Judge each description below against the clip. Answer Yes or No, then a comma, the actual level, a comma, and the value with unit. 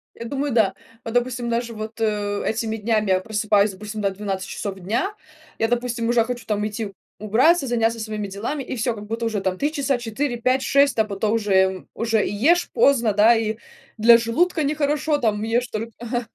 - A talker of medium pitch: No, high, 225 Hz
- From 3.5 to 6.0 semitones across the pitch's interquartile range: No, narrow, 2.6 semitones